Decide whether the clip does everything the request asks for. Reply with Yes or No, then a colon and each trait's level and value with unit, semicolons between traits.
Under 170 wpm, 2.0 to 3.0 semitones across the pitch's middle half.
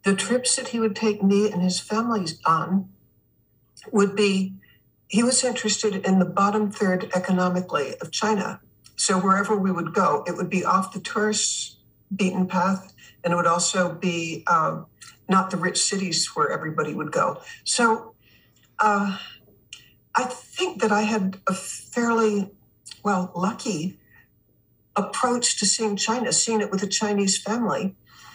Yes: average, 150 wpm; average, 2.7 semitones